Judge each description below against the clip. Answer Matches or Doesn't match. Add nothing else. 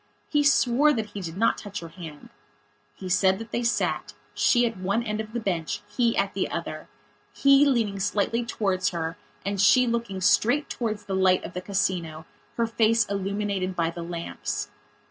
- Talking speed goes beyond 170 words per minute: Matches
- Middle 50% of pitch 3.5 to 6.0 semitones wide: Matches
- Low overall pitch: Doesn't match